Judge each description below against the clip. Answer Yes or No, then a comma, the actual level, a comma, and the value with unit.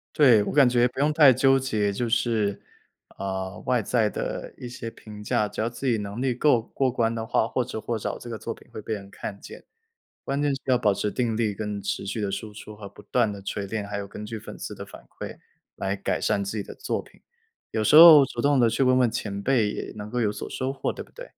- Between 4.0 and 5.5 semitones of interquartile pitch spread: No, average, 3.5 semitones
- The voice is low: Yes, low, 115 Hz